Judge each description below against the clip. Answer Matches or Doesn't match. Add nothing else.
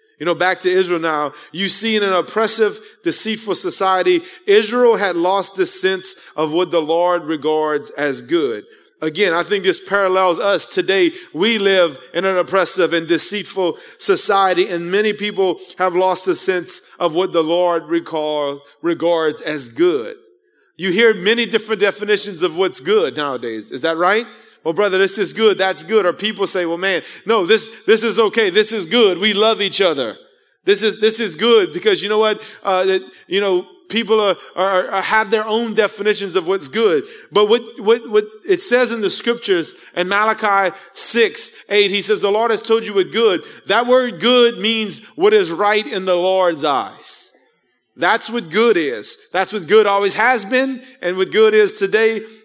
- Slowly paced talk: Doesn't match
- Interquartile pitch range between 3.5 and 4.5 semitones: Matches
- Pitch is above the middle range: Matches